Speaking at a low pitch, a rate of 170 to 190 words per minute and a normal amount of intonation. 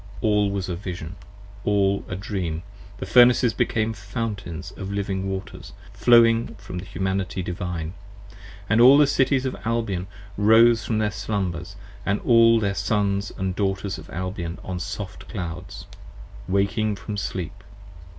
No: low, 100 Hz; average, 140 wpm; average, 3.0 semitones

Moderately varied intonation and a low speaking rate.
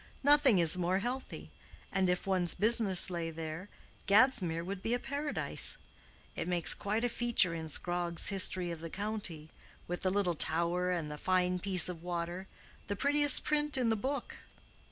No: average, 4.6 semitones; average, 165 wpm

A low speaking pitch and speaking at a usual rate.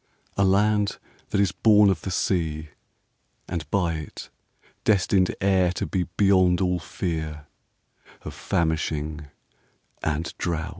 No: very low, 90 Hz; slow, 120 wpm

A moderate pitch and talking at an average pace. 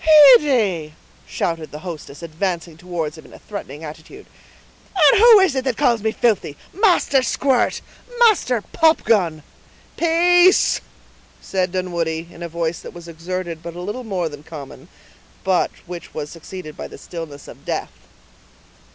Yes: medium, 180 Hz; average, 150 wpm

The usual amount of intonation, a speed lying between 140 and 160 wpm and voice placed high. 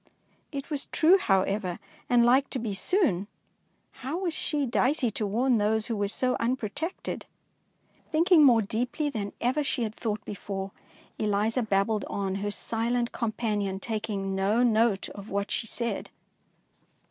Yes: average, 4.1 semitones; average, 145 wpm; high, 225 Hz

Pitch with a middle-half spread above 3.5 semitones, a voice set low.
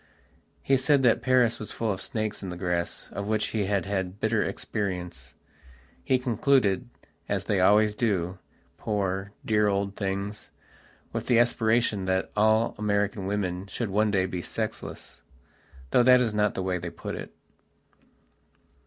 No: average, 2.7 semitones; low, 105 Hz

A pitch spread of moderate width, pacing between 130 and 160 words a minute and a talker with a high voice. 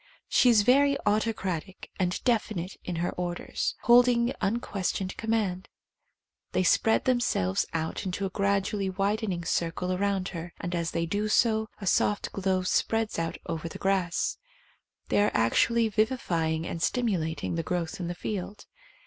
Yes: average, 4.0 semitones; average, 155 wpm; high, 195 Hz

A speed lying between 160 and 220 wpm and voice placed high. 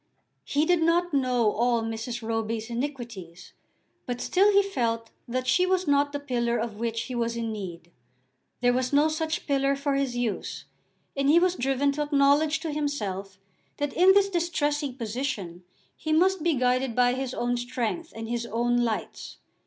Yes: average, 175 wpm; very high, 255 Hz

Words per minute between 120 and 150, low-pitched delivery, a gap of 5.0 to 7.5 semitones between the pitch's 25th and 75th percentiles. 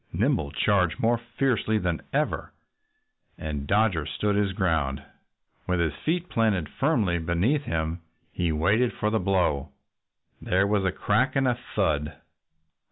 Yes: average, 140 wpm; very low, 95 Hz; wide, 5.4 semitones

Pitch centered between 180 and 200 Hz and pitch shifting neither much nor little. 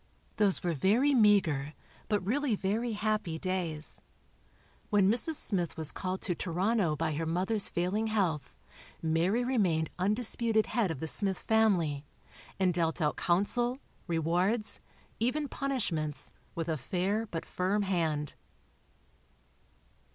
Yes: high, 190 Hz; average, 4.9 semitones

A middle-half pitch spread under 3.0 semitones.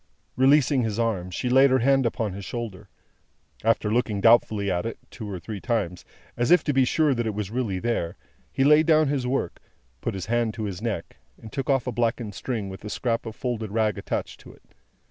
No: average, 3.7 semitones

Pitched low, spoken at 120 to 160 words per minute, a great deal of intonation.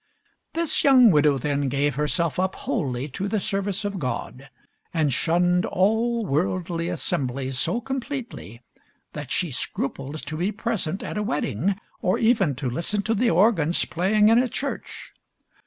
No: medium, 180 Hz; average, 155 wpm; wide, 6.8 semitones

